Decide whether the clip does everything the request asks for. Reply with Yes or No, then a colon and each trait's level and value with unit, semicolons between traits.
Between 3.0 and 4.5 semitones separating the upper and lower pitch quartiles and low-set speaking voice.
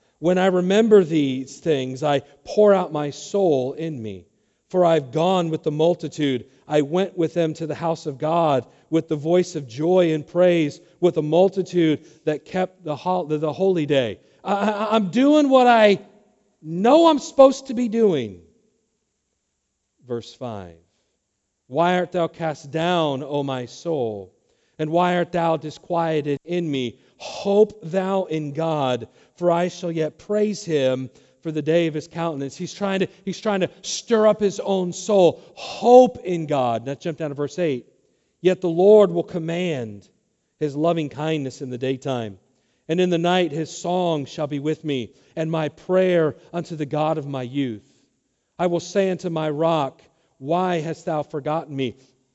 No: average, 3.9 semitones; medium, 165 Hz